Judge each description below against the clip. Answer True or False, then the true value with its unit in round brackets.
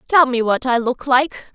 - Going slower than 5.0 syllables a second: True (4.4 syllables/s)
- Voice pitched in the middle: False (260 Hz)